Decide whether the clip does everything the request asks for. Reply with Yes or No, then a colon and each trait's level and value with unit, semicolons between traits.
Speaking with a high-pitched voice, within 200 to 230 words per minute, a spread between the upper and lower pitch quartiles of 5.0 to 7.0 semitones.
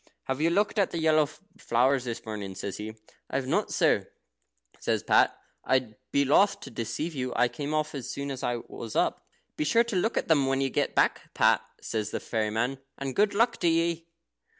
No: low, 135 Hz; fast, 205 wpm; wide, 5.6 semitones